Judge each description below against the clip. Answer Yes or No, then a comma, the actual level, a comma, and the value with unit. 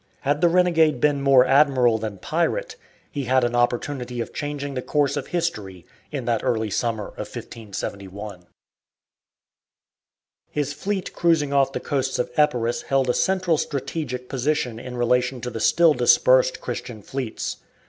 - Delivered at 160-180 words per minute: No, average, 150 wpm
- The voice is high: No, low, 130 Hz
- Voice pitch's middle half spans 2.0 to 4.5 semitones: Yes, average, 3.6 semitones